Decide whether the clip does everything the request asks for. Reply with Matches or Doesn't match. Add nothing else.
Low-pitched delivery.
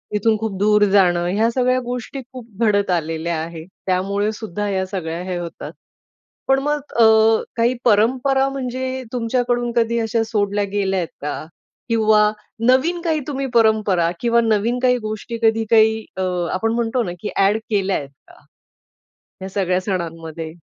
Doesn't match